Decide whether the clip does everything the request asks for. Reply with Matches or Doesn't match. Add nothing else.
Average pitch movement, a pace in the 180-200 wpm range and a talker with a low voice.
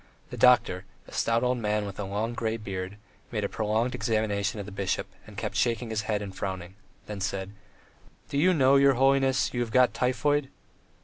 Matches